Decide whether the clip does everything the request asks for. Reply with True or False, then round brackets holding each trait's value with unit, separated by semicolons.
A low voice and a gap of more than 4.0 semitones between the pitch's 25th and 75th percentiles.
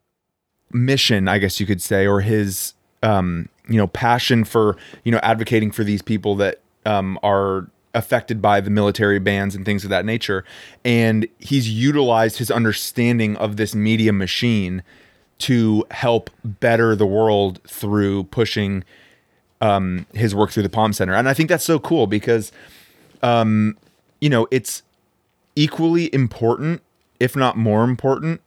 False (110 Hz; 2.8 semitones)